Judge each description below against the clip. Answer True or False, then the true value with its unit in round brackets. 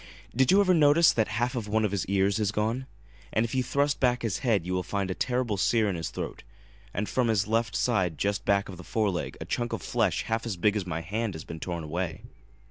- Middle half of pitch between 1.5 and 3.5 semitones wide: False (4.1 semitones)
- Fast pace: True (260 wpm)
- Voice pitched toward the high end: False (105 Hz)